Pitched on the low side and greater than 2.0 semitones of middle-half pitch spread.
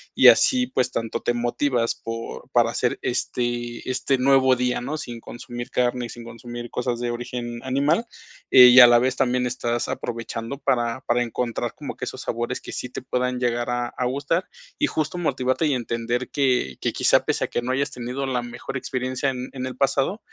No: low, 125 Hz; narrow, 1.7 semitones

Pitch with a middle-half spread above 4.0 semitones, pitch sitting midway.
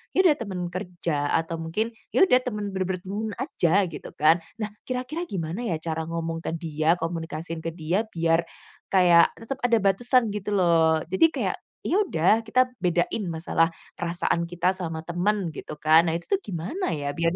Yes: average, 4.7 semitones; medium, 175 Hz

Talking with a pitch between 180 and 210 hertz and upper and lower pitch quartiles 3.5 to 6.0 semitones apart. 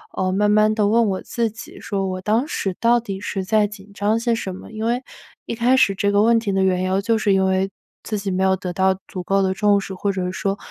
No: high, 200 Hz; narrow, 2.4 semitones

